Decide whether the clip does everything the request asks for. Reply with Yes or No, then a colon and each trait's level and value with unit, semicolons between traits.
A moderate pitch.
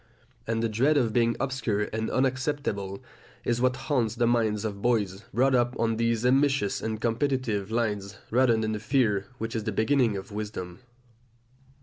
No: low, 115 Hz